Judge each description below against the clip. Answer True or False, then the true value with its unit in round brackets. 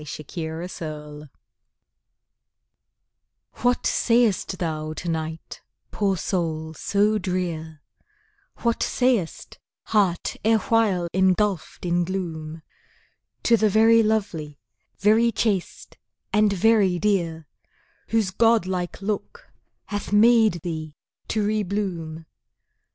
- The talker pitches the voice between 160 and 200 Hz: True (190 Hz)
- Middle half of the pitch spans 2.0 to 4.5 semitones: False (4.9 semitones)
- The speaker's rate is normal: False (95 wpm)